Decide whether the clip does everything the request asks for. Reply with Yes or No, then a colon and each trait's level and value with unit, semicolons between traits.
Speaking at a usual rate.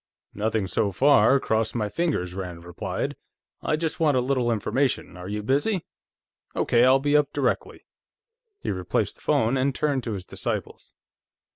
Yes: average, 160 wpm